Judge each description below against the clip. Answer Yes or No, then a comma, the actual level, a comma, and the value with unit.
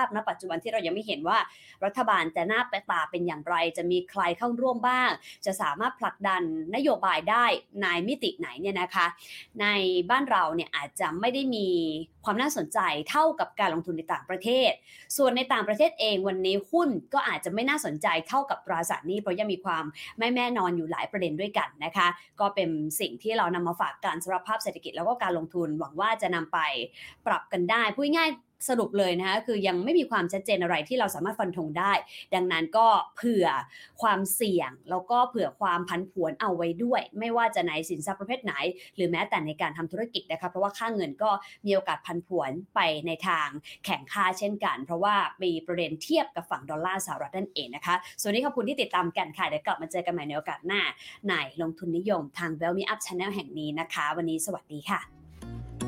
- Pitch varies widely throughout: No, average, 4.8 semitones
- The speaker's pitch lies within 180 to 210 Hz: Yes, medium, 185 Hz